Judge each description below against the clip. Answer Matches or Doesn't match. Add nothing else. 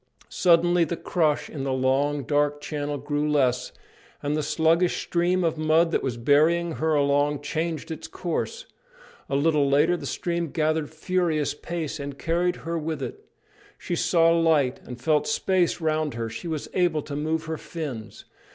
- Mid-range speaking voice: Matches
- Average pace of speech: Matches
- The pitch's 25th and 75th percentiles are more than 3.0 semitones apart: Doesn't match